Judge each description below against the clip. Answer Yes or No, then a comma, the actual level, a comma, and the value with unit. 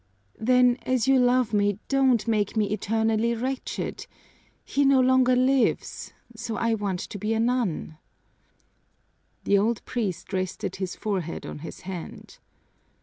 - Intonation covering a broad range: No, average, 3.8 semitones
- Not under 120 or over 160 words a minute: Yes, average, 140 wpm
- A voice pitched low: No, high, 225 Hz